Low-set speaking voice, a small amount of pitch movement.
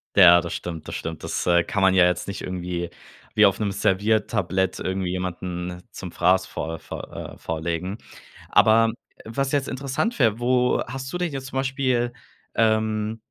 No: low, 100 Hz; wide, 5.4 semitones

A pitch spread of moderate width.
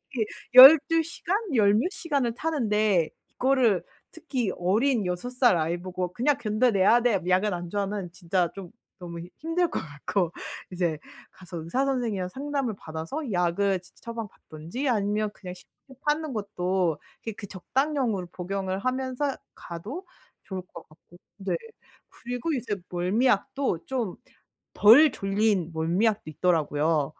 No: wide, 6.2 semitones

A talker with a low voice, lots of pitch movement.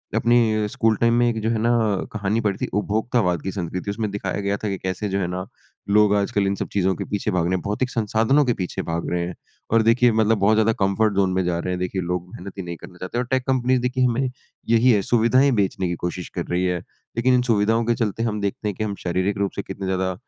No: low, 105 Hz; average, 3.6 semitones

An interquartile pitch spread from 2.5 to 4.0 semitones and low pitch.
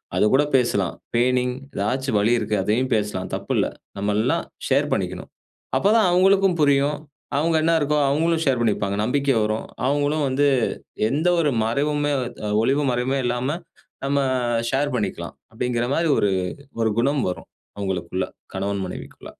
No: average, 5.2 semitones; low, 130 Hz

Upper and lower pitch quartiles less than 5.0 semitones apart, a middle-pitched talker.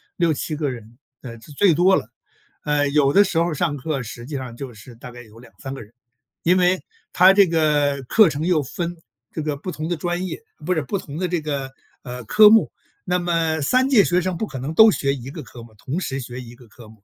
No: wide, 5.5 semitones; medium, 150 Hz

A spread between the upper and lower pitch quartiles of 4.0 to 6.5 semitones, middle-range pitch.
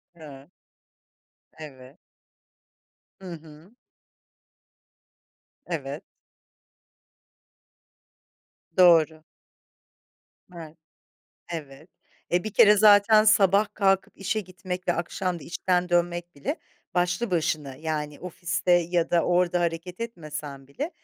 No: average, 3.2 semitones; medium, 175 Hz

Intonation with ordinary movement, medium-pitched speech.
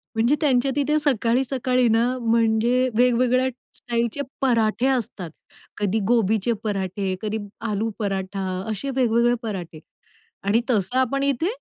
No: average, 3.2 semitones; high, 235 Hz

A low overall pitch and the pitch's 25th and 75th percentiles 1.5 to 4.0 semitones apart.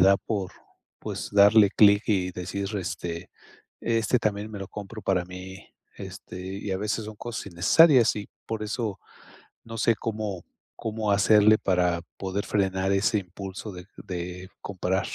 Yes: low, 100 Hz; narrow, 2.5 semitones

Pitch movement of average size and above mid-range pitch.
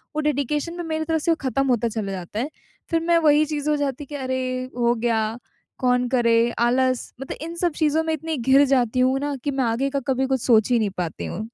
Yes: average, 3.9 semitones; very high, 265 Hz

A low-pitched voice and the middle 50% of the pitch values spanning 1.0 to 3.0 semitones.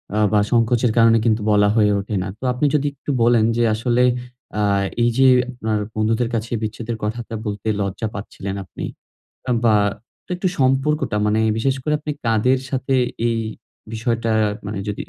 Yes: low, 115 Hz; average, 2.7 semitones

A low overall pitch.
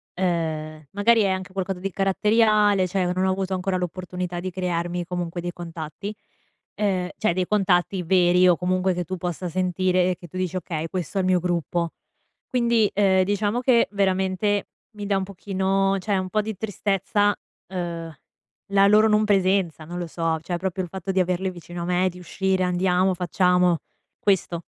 No: medium, 185 Hz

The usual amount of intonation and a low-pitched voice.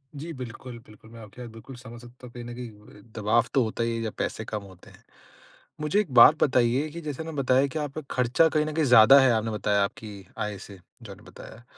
Yes: average, 3.9 semitones; low, 120 Hz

